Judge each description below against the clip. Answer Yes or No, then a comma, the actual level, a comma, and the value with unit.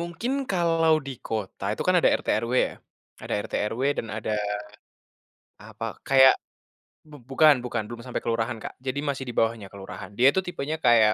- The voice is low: Yes, low, 125 Hz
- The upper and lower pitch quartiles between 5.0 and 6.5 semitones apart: Yes, wide, 5.5 semitones